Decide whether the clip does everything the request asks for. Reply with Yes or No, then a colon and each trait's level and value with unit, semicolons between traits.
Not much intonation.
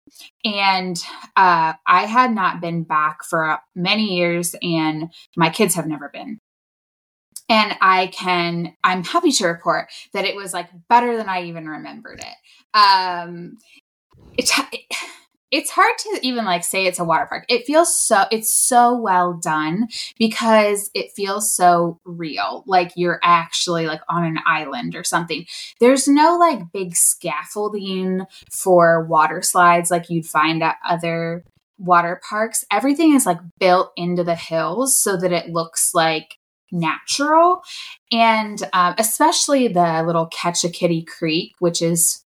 No: wide, 5.5 semitones